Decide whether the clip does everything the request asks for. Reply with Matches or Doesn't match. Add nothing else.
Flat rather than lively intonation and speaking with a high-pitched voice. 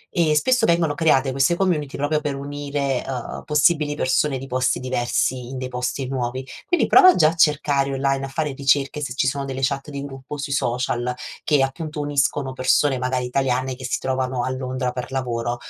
Doesn't match